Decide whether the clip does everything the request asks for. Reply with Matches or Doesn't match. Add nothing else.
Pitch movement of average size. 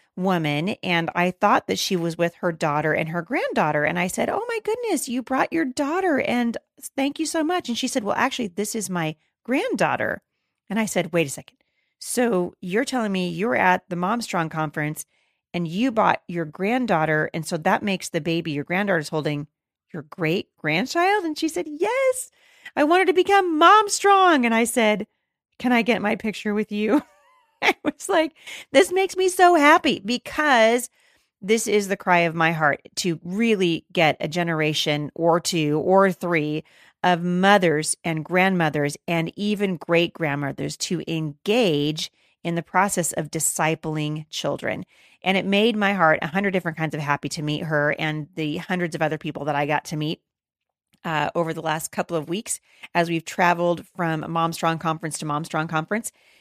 Doesn't match